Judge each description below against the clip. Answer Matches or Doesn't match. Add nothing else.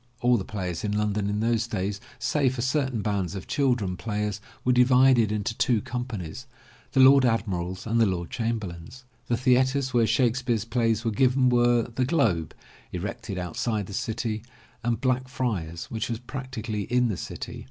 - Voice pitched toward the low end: Matches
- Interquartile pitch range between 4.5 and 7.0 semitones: Doesn't match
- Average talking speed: Matches